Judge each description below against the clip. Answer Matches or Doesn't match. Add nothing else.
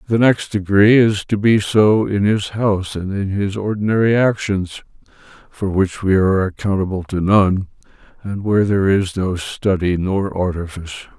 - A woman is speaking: Doesn't match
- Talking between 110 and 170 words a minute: Matches